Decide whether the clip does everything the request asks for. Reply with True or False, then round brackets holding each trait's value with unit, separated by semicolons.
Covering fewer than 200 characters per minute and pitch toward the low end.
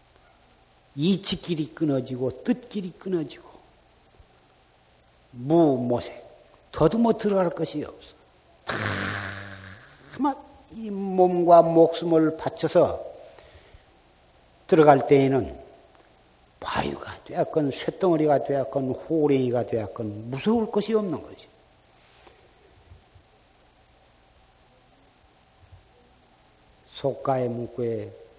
False (170 characters per minute; 150 Hz)